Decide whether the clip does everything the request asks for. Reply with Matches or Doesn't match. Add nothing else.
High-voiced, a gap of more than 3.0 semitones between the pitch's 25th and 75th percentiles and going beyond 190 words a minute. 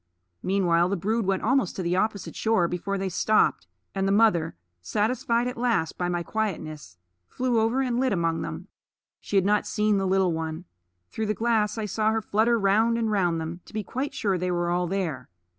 Matches